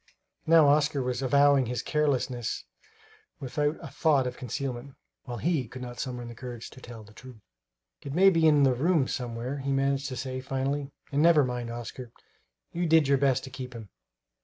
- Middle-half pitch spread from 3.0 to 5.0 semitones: No, narrow, 2.6 semitones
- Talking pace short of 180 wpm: No, average, 185 wpm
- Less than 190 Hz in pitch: Yes, low, 135 Hz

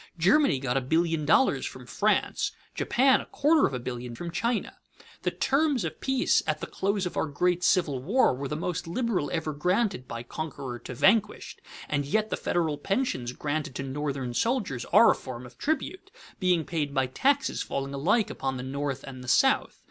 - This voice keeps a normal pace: Yes, average, 190 wpm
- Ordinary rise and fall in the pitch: No, wide, 7.9 semitones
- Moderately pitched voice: Yes, medium, 155 Hz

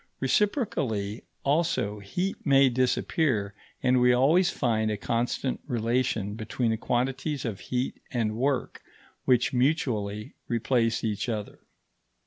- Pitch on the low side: Yes, low, 125 Hz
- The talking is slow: Yes, slow, 115 wpm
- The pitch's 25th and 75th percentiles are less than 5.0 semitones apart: Yes, average, 3.6 semitones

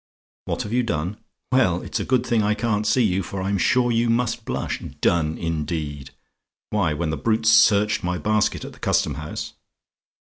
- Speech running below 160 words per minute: No, average, 185 wpm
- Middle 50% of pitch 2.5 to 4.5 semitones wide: No, wide, 5.4 semitones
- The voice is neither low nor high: No, low, 100 Hz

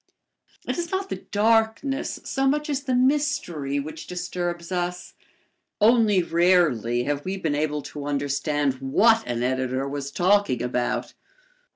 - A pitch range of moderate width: No, wide, 7.9 semitones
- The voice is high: No, medium, 175 Hz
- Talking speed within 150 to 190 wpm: No, average, 140 wpm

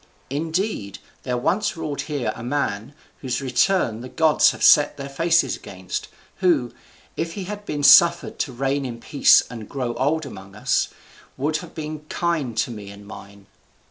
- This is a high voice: No, medium, 140 Hz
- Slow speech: No, average, 170 wpm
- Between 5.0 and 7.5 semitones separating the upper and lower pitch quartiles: Yes, average, 5.3 semitones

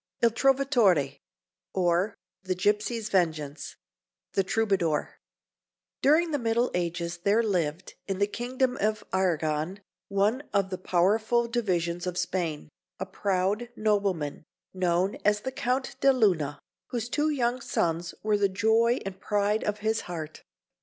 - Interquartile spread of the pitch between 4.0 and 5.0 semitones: Yes, average, 4.5 semitones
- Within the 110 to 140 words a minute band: Yes, slow, 135 wpm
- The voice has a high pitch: Yes, high, 200 Hz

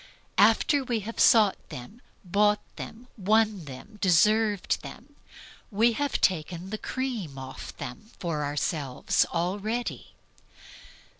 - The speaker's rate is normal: No, slow, 115 wpm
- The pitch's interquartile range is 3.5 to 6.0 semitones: Yes, average, 5.1 semitones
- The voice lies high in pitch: Yes, high, 205 Hz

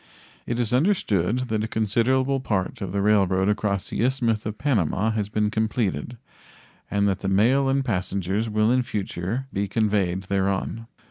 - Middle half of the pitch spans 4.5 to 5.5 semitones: No, average, 3.5 semitones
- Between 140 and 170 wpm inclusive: Yes, average, 160 wpm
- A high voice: No, low, 105 Hz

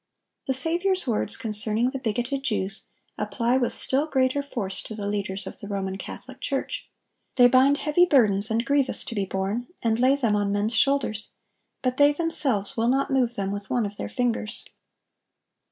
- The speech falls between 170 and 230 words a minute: Yes, average, 180 wpm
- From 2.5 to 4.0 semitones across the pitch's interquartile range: No, average, 4.7 semitones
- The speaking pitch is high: Yes, high, 240 Hz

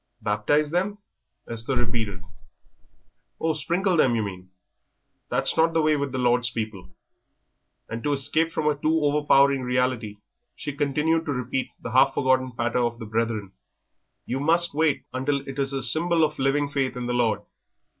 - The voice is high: No, low, 135 Hz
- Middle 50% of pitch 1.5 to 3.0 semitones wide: No, average, 4.0 semitones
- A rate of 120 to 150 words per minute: No, average, 165 wpm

